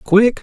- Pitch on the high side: Yes, high, 215 Hz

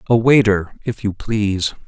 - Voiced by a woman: No, male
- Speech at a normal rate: Yes, average, 160 wpm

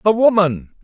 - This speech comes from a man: Yes, male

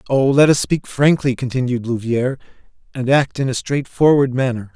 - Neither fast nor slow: Yes, average, 165 wpm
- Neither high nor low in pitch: No, low, 130 Hz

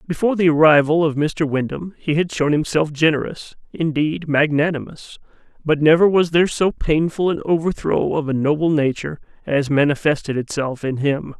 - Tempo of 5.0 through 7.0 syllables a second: Yes, 5.2 syllables/s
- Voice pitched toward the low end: No, medium, 155 Hz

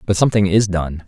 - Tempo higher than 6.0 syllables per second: Yes, 6.3 syllables/s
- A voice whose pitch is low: Yes, very low, 95 Hz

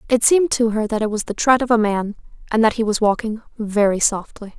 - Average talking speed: No, fast, 250 wpm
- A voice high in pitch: Yes, high, 220 Hz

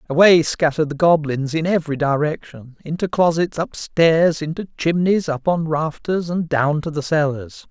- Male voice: Yes, male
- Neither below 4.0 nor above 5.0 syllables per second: Yes, 4.7 syllables/s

